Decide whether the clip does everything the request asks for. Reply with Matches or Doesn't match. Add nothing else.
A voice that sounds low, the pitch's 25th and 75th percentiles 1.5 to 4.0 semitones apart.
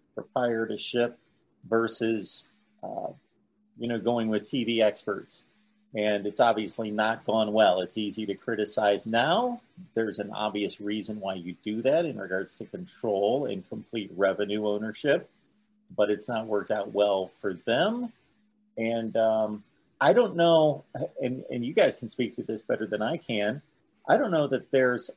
Matches